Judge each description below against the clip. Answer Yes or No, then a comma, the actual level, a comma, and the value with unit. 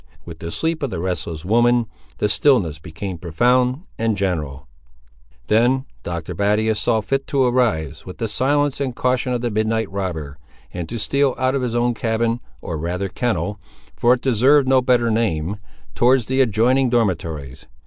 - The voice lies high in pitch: No, low, 115 Hz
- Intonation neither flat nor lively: No, wide, 5.8 semitones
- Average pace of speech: Yes, average, 170 wpm